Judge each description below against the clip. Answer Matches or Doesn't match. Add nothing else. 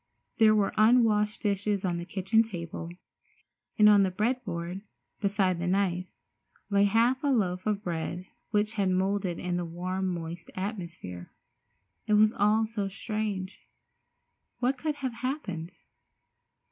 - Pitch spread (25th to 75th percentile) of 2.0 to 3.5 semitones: Matches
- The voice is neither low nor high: Doesn't match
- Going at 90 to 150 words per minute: Matches